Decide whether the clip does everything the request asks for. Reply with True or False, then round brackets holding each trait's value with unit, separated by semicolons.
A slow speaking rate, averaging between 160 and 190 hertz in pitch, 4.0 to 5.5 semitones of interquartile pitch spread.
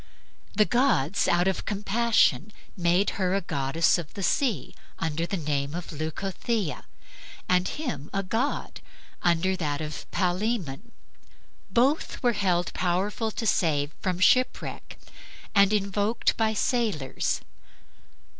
True (125 wpm; 185 Hz; 4.8 semitones)